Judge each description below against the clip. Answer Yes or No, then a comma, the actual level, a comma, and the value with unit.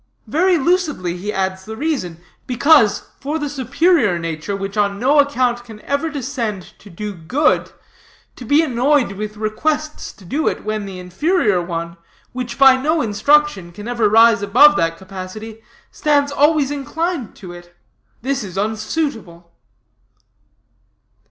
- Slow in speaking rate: No, average, 145 wpm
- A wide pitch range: Yes, wide, 6.7 semitones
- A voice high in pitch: Yes, high, 230 Hz